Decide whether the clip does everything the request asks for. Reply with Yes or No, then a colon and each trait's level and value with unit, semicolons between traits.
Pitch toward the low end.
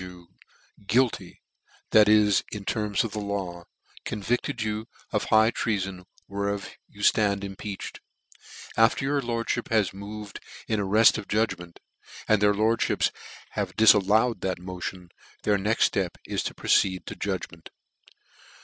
Yes: low, 105 Hz